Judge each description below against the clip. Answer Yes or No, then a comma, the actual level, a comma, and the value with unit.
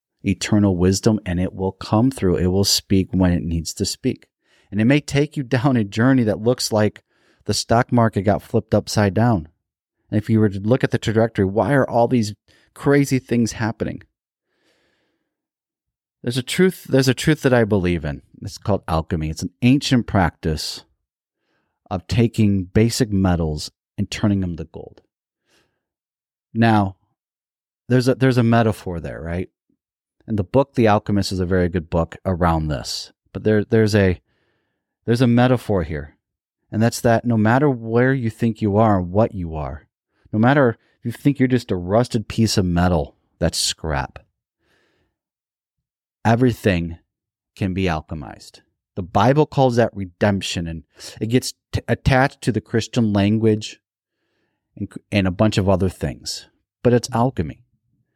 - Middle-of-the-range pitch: No, low, 105 Hz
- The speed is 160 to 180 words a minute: Yes, average, 165 wpm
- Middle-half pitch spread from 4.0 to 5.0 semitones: Yes, average, 4.3 semitones